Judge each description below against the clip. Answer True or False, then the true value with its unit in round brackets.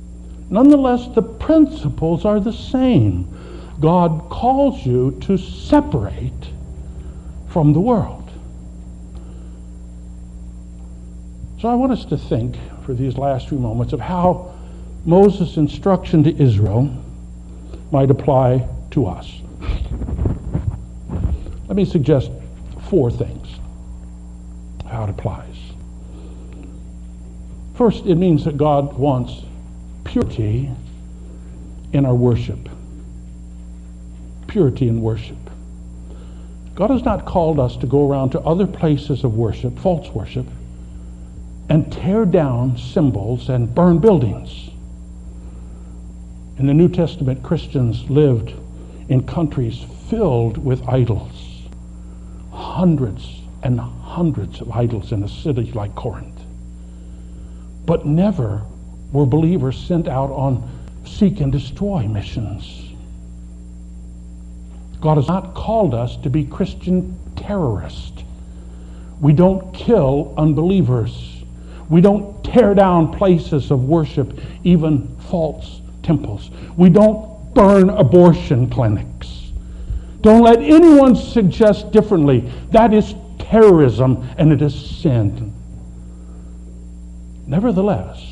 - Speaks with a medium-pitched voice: False (110 Hz)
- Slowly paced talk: True (105 wpm)